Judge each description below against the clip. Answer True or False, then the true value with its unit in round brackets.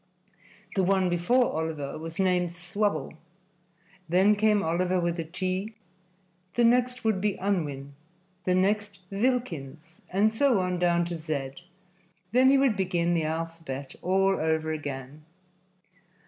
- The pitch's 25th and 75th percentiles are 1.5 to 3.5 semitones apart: False (4.1 semitones)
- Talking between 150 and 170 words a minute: False (135 wpm)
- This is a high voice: False (180 Hz)